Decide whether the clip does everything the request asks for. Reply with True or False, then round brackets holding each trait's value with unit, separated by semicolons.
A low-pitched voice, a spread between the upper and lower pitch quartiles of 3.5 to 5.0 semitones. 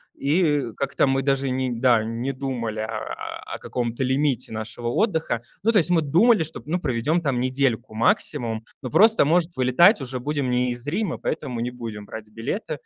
True (130 Hz; 4.5 semitones)